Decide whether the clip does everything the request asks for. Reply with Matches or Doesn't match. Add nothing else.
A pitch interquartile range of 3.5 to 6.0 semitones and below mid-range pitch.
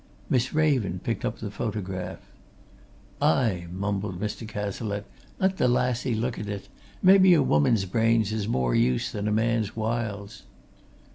Doesn't match